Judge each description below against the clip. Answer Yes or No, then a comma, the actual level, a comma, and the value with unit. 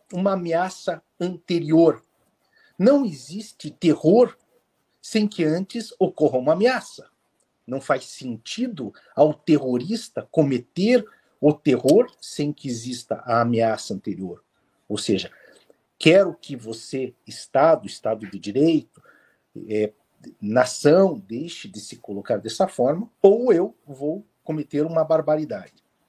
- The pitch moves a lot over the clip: Yes, wide, 7.6 semitones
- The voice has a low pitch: No, medium, 155 Hz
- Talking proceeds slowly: Yes, slow, 115 wpm